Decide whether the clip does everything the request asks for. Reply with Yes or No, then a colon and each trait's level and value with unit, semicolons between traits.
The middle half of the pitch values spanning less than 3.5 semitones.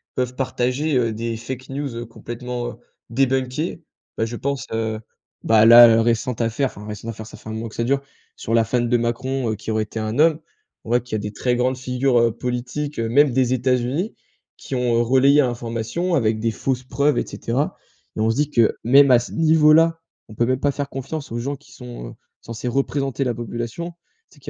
Yes: average, 2.9 semitones